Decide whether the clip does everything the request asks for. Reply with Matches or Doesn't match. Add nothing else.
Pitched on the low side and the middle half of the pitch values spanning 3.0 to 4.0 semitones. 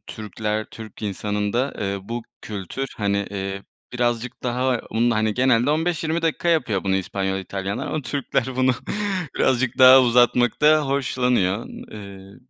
Doesn't match